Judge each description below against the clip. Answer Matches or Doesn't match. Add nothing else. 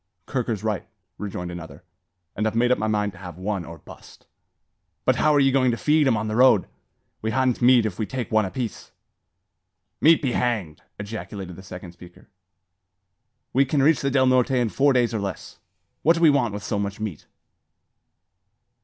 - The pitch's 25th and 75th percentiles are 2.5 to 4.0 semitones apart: Doesn't match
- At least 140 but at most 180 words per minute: Doesn't match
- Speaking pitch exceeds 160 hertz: Doesn't match